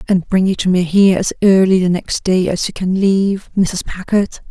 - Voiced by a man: No, female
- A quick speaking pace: Yes, fast, 225 wpm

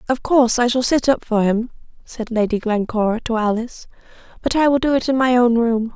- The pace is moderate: No, fast, 220 wpm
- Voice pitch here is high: Yes, high, 235 Hz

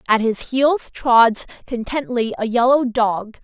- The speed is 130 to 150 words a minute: Yes, average, 140 wpm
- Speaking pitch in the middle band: No, high, 240 Hz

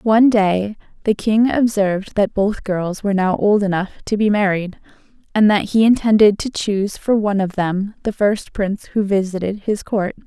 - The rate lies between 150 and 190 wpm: Yes, average, 185 wpm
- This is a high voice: Yes, high, 205 Hz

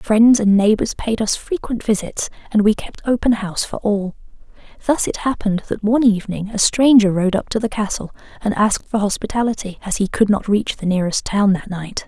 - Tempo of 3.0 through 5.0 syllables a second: No, 5.6 syllables/s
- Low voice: No, high, 210 Hz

